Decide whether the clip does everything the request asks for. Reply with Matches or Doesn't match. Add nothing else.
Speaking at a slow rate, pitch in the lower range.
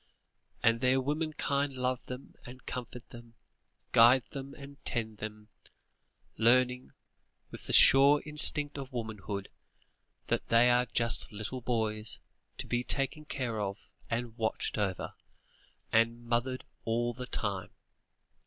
Matches